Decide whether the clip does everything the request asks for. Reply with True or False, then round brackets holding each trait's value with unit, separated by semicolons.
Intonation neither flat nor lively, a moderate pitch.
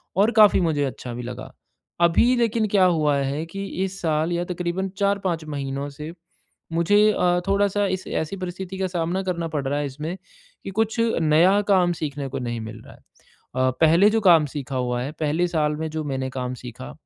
True (5.0 semitones; 165 Hz)